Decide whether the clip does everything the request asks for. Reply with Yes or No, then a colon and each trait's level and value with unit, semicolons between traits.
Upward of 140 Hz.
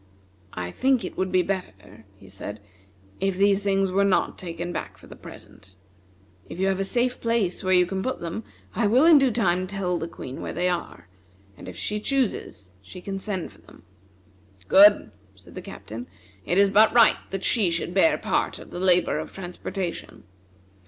Yes: medium, 185 Hz